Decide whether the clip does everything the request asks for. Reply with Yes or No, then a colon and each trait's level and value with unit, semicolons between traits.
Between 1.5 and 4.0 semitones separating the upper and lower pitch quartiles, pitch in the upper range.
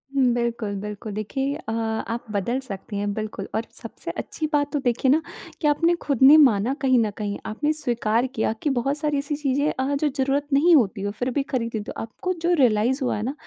No: average, 4.6 semitones; very high, 255 Hz